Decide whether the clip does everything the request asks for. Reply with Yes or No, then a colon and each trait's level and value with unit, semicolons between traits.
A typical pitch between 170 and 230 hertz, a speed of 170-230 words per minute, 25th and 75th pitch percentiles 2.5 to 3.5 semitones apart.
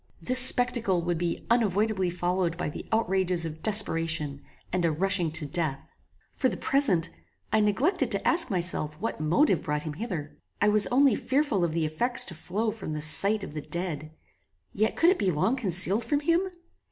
No: medium, 185 Hz; average, 185 wpm; wide, 5.6 semitones